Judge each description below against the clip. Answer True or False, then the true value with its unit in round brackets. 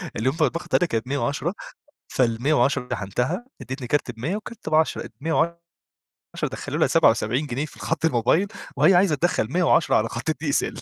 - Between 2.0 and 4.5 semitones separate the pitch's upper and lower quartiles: False (5.3 semitones)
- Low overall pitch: False (145 Hz)